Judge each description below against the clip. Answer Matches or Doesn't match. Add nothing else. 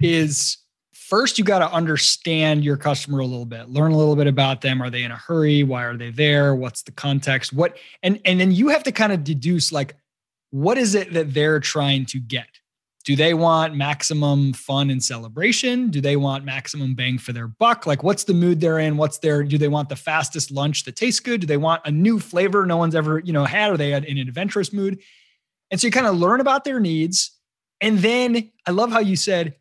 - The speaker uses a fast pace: Matches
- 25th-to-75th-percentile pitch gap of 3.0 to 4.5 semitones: Doesn't match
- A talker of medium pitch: Matches